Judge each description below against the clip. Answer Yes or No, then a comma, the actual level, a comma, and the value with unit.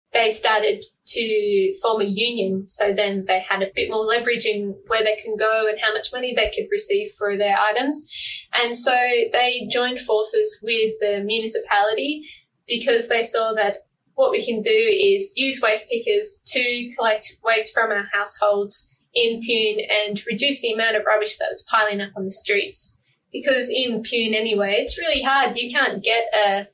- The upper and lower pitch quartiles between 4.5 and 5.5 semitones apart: Yes, average, 4.8 semitones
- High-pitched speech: Yes, high, 230 Hz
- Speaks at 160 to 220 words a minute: Yes, average, 180 wpm